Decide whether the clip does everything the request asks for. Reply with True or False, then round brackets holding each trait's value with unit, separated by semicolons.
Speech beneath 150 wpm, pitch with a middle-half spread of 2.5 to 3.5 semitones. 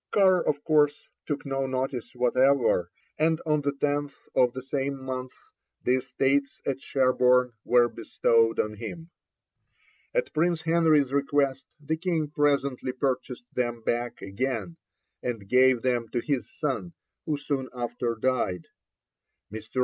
True (135 wpm; 2.8 semitones)